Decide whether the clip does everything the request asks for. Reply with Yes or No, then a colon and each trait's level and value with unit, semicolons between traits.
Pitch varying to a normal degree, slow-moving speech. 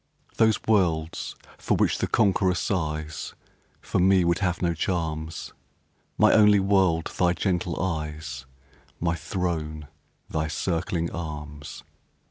Yes: average, 3.2 semitones; slow, 115 wpm